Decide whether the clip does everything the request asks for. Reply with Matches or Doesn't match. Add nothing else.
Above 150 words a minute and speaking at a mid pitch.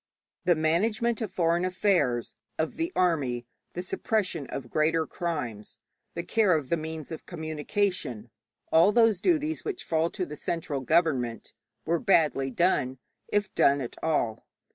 Doesn't match